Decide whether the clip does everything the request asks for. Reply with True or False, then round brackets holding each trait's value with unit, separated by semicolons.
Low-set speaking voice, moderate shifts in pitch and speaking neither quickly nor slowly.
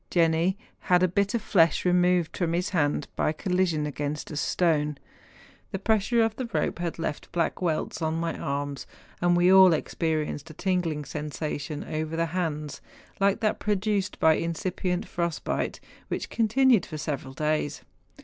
False (170 Hz; 3.5 semitones; 165 wpm)